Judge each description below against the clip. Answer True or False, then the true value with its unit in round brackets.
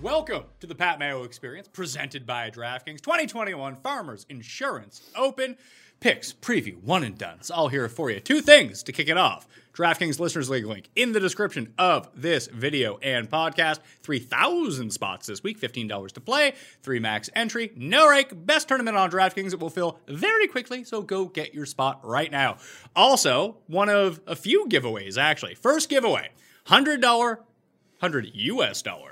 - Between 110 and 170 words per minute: False (180 wpm)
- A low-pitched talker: False (180 Hz)